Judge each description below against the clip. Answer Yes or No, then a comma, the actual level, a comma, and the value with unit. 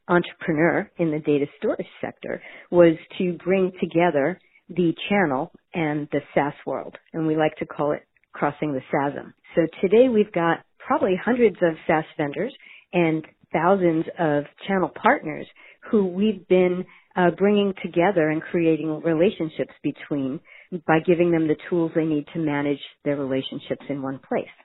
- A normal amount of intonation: Yes, average, 3.2 semitones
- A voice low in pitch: No, medium, 165 Hz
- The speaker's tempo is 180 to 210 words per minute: No, average, 155 wpm